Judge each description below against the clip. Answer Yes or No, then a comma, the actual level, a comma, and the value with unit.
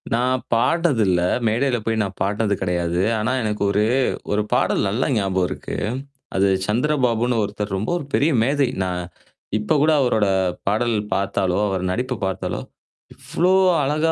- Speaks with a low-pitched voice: Yes, low, 110 Hz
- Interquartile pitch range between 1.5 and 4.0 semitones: No, average, 4.7 semitones